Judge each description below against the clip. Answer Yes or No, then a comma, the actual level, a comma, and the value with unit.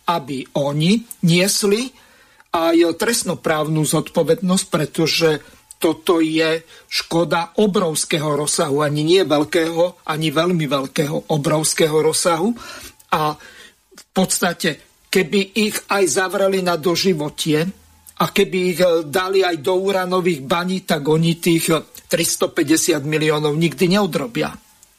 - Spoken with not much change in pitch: No, average, 3.1 semitones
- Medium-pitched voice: Yes, medium, 170 Hz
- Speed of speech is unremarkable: No, slow, 105 wpm